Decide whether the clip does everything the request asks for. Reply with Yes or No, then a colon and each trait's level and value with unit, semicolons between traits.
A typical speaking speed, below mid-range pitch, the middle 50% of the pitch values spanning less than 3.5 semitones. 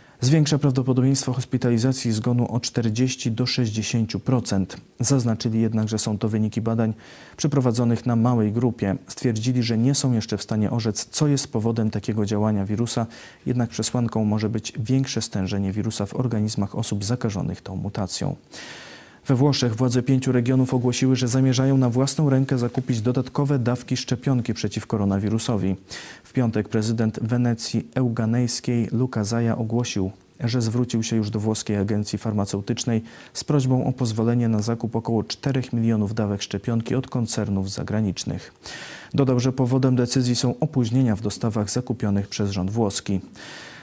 Yes: average, 145 wpm; low, 115 Hz; average, 2.8 semitones